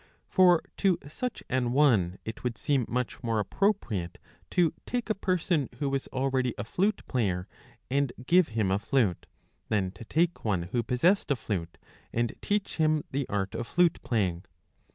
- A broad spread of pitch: Yes, wide, 7.5 semitones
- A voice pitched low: Yes, low, 125 Hz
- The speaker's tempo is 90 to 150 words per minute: No, average, 170 wpm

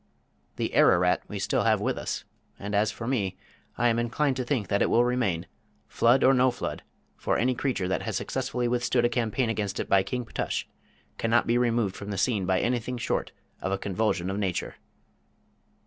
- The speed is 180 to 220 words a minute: Yes, average, 195 wpm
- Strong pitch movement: No, average, 3.9 semitones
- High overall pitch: No, low, 115 Hz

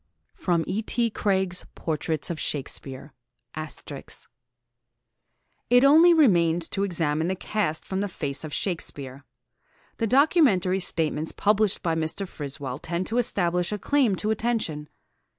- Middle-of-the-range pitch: Yes, medium, 175 Hz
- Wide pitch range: Yes, wide, 5.9 semitones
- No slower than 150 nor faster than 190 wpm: No, slow, 135 wpm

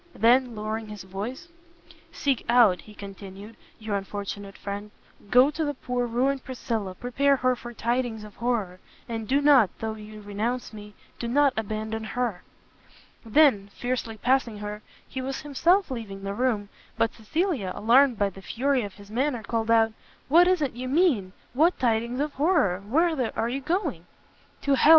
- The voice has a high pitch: Yes, high, 235 Hz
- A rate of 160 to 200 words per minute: Yes, average, 170 wpm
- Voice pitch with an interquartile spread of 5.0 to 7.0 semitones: No, average, 4.2 semitones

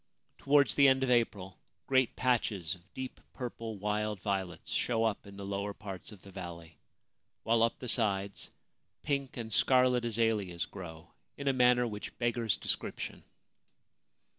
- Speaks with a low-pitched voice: Yes, low, 110 Hz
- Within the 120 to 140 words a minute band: No, average, 150 wpm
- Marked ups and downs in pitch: No, average, 4.0 semitones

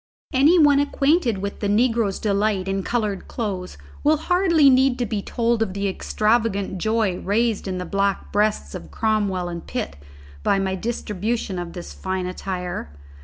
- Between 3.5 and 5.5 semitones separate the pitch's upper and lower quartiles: Yes, average, 4.0 semitones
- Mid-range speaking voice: No, high, 205 Hz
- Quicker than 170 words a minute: No, average, 165 wpm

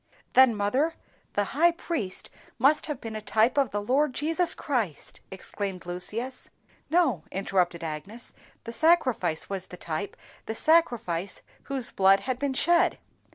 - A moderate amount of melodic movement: No, wide, 6.9 semitones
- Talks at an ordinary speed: Yes, average, 150 wpm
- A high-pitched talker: Yes, high, 230 Hz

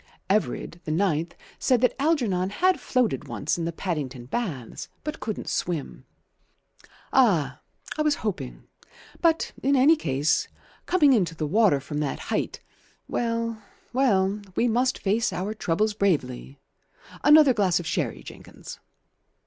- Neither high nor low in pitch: No, high, 200 Hz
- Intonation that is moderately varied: No, wide, 7.8 semitones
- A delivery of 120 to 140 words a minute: Yes, slow, 135 wpm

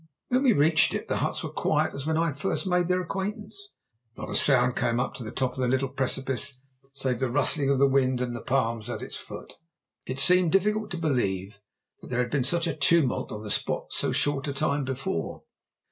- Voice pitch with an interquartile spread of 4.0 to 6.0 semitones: Yes, average, 4.9 semitones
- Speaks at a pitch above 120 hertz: Yes, medium, 140 Hz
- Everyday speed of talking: No, fast, 230 wpm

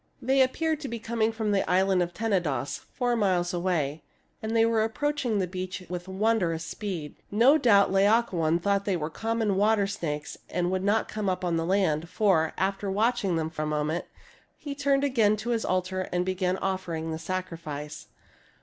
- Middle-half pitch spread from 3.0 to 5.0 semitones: Yes, average, 4.3 semitones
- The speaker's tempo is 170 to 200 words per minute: Yes, average, 180 wpm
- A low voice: No, high, 190 Hz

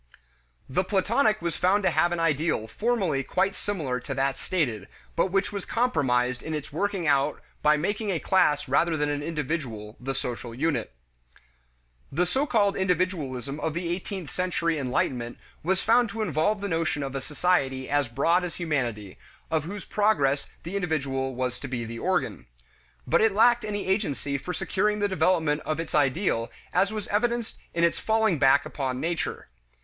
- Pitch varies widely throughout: Yes, wide, 6.2 semitones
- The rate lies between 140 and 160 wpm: No, average, 175 wpm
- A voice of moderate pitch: Yes, medium, 165 Hz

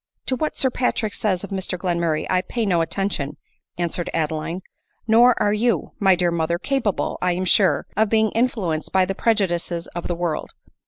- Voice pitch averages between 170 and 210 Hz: Yes, medium, 185 Hz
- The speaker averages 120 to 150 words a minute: No, average, 195 wpm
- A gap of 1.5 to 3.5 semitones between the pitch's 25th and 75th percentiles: No, average, 4.2 semitones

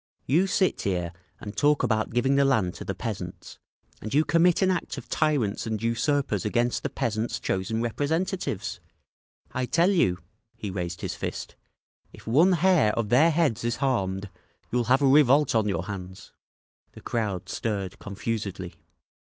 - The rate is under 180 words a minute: Yes, average, 160 wpm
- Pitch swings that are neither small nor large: No, wide, 6.4 semitones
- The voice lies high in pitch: No, low, 115 Hz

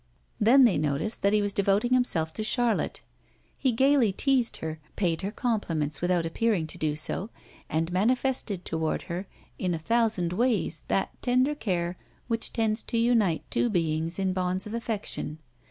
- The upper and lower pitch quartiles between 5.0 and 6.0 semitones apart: Yes, wide, 5.5 semitones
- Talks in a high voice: Yes, high, 200 Hz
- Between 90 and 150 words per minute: No, average, 165 wpm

